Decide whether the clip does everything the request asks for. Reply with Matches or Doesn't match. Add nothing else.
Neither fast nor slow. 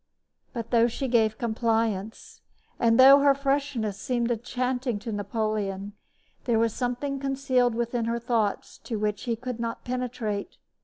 Matches